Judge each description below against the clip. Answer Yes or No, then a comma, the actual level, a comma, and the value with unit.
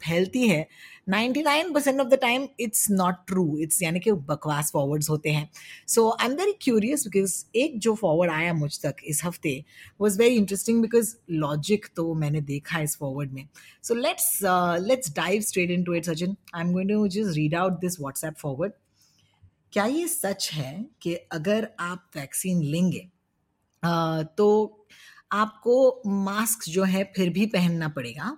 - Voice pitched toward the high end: No, medium, 180 Hz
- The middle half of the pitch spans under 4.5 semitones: No, wide, 5.6 semitones